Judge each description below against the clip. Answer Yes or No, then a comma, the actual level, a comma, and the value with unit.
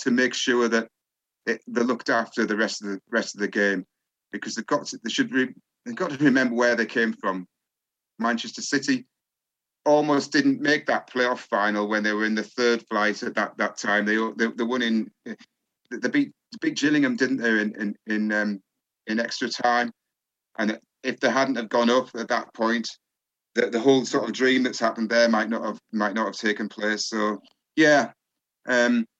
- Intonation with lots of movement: No, average, 3.0 semitones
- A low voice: Yes, low, 115 Hz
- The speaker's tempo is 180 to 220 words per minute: Yes, average, 200 wpm